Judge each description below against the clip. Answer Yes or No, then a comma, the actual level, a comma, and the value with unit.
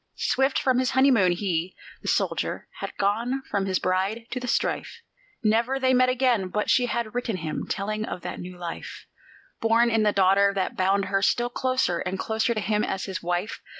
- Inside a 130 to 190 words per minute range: No, average, 200 wpm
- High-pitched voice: Yes, high, 215 Hz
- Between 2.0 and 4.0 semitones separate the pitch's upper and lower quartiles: No, average, 4.5 semitones